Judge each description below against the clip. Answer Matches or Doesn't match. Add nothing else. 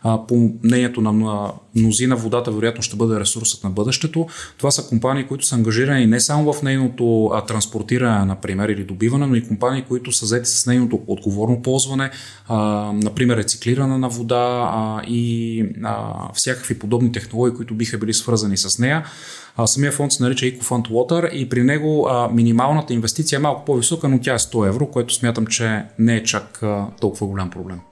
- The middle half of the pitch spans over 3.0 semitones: Doesn't match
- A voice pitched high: Doesn't match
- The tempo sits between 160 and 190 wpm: Matches